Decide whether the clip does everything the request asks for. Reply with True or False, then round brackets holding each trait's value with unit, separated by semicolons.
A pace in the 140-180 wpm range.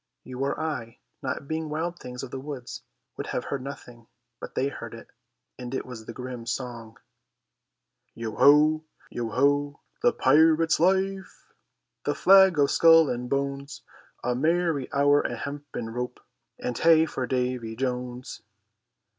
True (150 wpm)